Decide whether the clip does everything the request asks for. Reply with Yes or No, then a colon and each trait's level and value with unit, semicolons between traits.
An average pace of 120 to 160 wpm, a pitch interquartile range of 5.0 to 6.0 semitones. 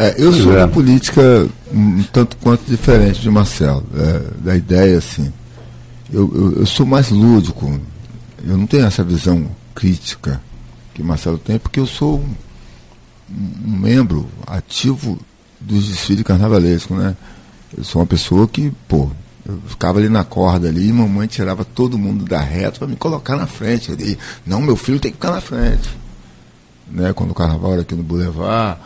No: average, 170 wpm; wide, 5.5 semitones